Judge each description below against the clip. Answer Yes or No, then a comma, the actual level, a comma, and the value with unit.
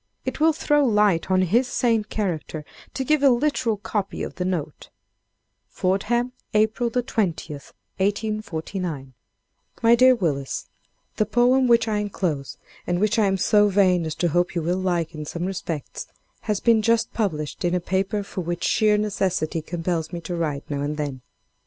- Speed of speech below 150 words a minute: No, average, 165 wpm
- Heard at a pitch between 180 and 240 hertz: Yes, high, 190 Hz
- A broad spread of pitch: No, average, 4.7 semitones